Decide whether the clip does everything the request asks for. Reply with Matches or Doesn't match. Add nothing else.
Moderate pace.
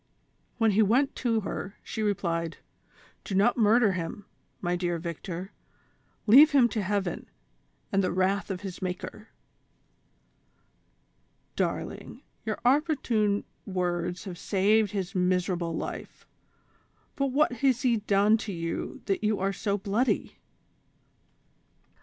Doesn't match